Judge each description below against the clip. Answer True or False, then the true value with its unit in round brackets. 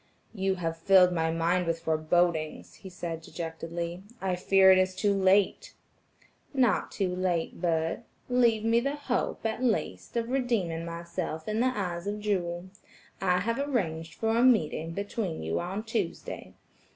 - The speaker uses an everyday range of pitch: True (4.6 semitones)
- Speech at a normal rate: True (155 wpm)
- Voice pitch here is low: False (185 Hz)